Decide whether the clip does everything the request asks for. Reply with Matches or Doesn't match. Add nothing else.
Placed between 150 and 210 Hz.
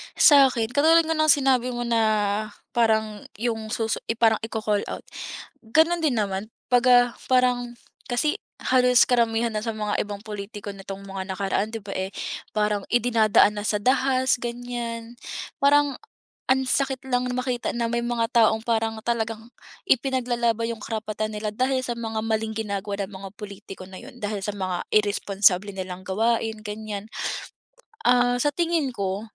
Doesn't match